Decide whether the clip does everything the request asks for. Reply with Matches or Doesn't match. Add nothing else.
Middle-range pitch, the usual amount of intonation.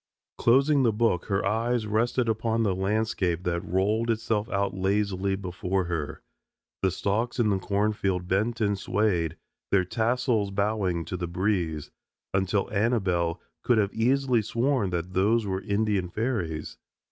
Doesn't match